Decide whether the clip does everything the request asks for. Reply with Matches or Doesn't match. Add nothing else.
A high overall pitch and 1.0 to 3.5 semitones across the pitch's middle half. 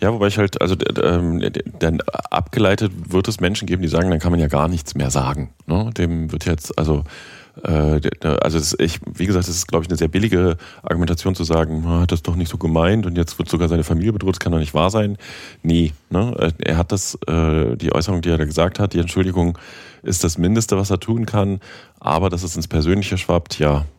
Doesn't match